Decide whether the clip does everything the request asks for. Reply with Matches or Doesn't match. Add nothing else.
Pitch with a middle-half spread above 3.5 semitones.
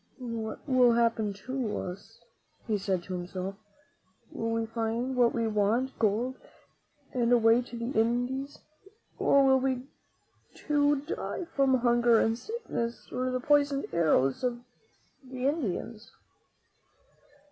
Doesn't match